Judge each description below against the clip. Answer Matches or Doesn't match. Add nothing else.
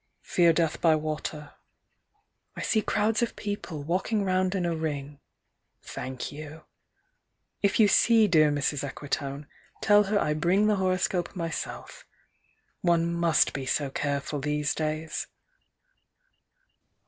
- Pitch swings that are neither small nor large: Matches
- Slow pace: Matches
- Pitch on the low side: Doesn't match